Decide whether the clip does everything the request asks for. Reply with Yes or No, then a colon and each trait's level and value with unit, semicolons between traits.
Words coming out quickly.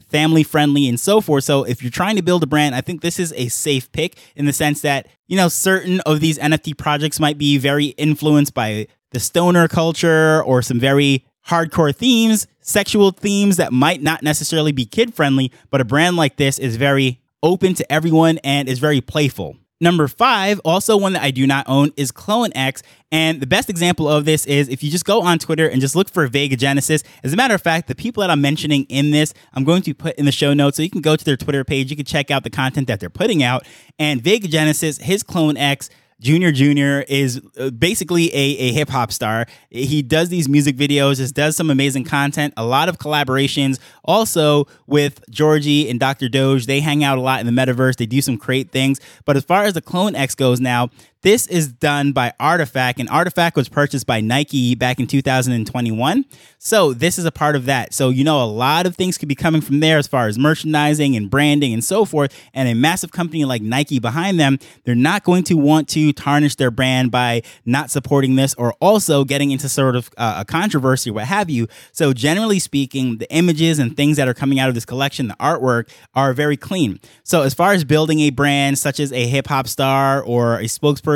Yes: fast, 225 wpm